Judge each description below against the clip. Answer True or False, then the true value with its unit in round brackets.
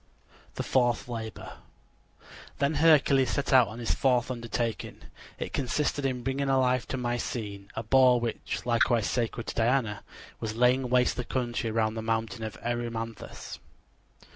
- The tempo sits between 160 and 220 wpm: False (145 wpm)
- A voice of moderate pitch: False (120 Hz)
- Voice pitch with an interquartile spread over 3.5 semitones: False (2.4 semitones)